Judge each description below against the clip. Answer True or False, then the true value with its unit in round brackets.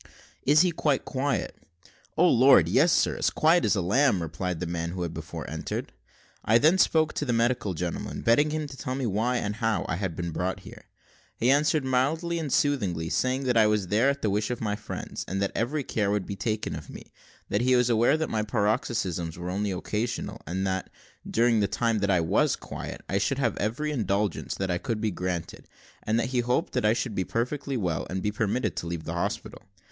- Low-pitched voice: True (110 Hz)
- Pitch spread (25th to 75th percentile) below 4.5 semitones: False (5.5 semitones)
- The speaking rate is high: True (220 wpm)